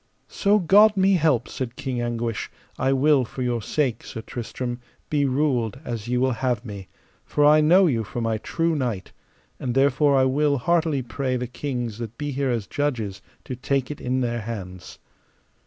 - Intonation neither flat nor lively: Yes, average, 3.8 semitones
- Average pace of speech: Yes, average, 185 wpm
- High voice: No, low, 130 Hz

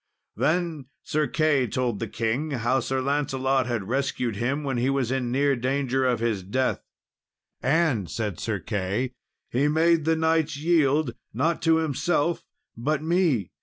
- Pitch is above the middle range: No, low, 135 Hz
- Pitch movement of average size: Yes, average, 4.4 semitones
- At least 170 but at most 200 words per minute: No, average, 155 wpm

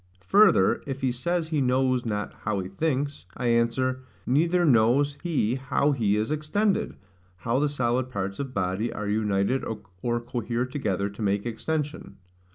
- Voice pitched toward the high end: No, low, 125 Hz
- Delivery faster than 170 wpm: No, average, 160 wpm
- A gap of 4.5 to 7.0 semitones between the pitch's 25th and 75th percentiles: Yes, average, 5.0 semitones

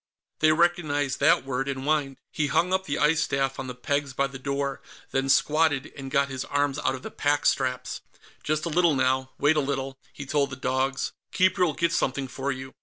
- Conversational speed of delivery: No, fast, 210 wpm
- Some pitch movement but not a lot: No, narrow, 2.3 semitones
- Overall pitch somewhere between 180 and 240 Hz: No, medium, 140 Hz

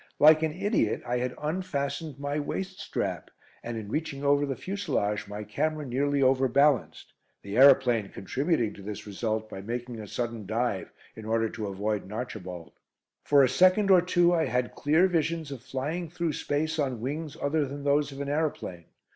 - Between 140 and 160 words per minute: No, average, 180 wpm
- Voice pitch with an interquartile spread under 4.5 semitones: No, wide, 5.6 semitones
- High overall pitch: No, medium, 140 Hz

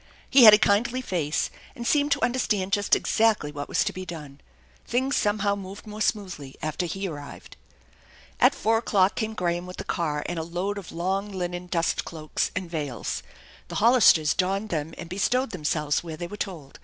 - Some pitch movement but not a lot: Yes, average, 4.3 semitones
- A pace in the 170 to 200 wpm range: Yes, average, 190 wpm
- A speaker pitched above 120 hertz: Yes, medium, 185 Hz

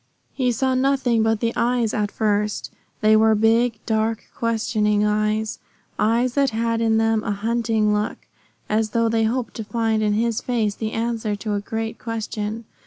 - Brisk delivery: No, average, 175 wpm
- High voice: Yes, high, 225 Hz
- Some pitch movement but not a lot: No, narrow, 1.4 semitones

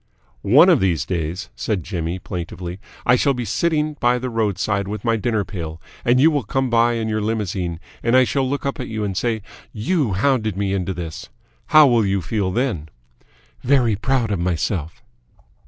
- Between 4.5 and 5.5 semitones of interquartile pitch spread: Yes, average, 5.1 semitones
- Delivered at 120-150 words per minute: No, average, 190 wpm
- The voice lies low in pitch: Yes, low, 110 Hz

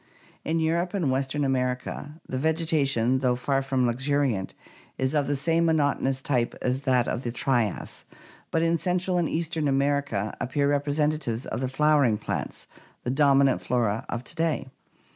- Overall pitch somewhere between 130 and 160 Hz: Yes, medium, 140 Hz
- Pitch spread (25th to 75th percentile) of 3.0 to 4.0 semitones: Yes, average, 3.3 semitones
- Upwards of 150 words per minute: Yes, average, 160 wpm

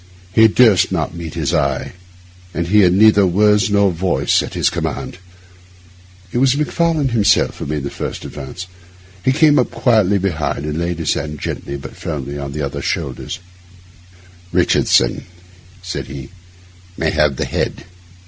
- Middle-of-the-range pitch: No, very low, 90 Hz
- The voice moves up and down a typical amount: No, wide, 6.2 semitones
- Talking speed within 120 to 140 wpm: No, average, 160 wpm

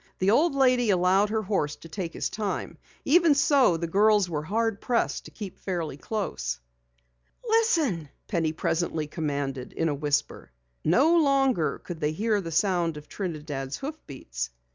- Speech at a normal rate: Yes, average, 155 wpm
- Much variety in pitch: Yes, wide, 6.9 semitones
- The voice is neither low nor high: Yes, medium, 180 Hz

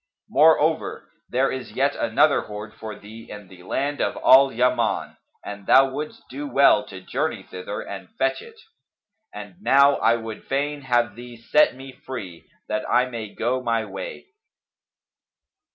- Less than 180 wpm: Yes, average, 155 wpm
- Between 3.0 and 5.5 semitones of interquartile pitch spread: Yes, average, 4.3 semitones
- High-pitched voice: No, low, 125 Hz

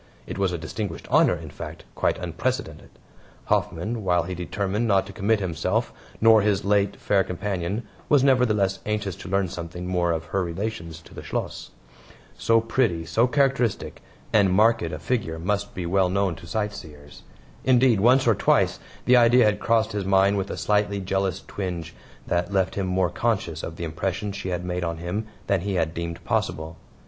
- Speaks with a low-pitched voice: Yes, very low, 95 Hz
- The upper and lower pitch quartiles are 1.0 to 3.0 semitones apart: No, average, 3.7 semitones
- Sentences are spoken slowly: No, average, 180 wpm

